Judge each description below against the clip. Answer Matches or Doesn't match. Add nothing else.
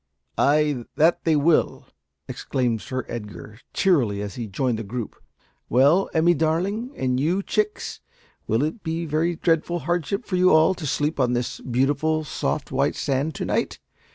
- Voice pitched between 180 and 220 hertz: Doesn't match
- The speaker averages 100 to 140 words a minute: Doesn't match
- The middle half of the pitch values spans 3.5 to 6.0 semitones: Matches